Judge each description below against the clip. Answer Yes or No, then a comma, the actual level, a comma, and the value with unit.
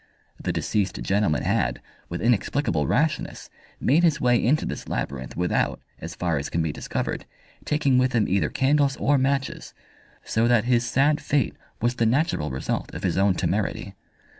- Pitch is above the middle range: No, low, 120 Hz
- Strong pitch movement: Yes, wide, 7.7 semitones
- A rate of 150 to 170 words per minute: Yes, average, 165 wpm